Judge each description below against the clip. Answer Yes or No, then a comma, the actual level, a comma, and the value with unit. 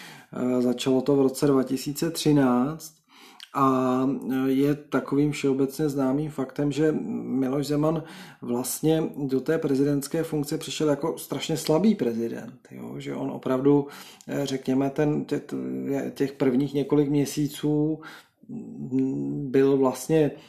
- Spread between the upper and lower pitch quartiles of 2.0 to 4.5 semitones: Yes, narrow, 2.3 semitones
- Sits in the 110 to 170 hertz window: Yes, medium, 140 Hz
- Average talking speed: No, slow, 110 wpm